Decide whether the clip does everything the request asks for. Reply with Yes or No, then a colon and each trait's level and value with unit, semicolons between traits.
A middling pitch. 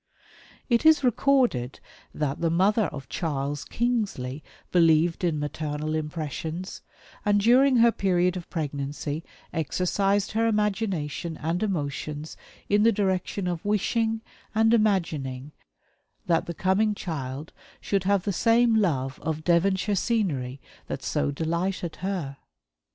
Yes: medium, 175 Hz